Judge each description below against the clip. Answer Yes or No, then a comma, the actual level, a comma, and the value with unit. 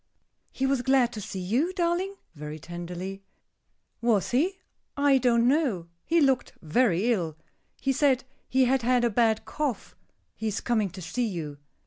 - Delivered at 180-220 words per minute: No, average, 160 wpm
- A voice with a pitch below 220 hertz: No, high, 240 Hz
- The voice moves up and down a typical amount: No, wide, 6.1 semitones